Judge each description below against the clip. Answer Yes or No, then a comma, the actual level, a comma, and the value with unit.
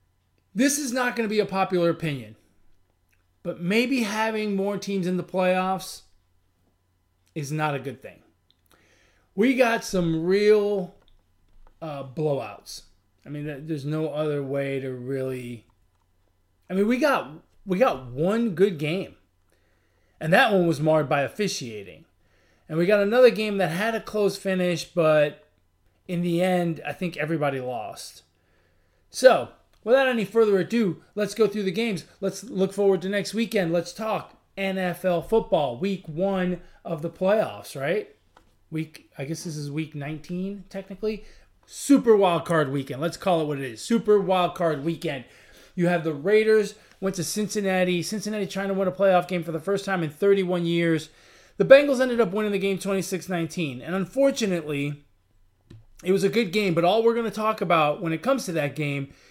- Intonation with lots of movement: Yes, wide, 6.1 semitones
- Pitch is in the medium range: Yes, medium, 175 Hz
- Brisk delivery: No, average, 170 wpm